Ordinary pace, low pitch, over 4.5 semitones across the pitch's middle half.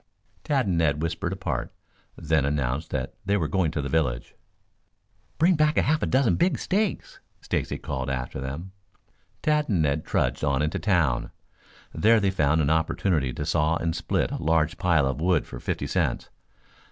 Yes: average, 175 wpm; very low, 80 Hz; wide, 5.4 semitones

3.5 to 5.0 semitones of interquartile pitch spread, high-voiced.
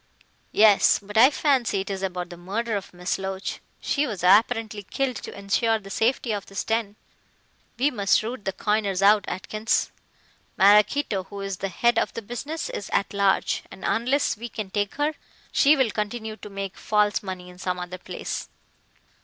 No: average, 3.0 semitones; high, 205 Hz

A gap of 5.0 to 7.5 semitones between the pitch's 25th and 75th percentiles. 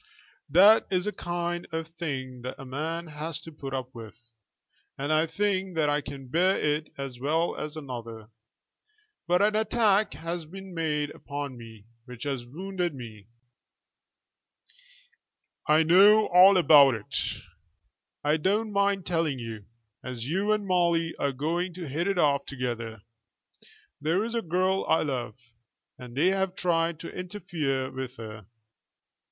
Yes: wide, 5.4 semitones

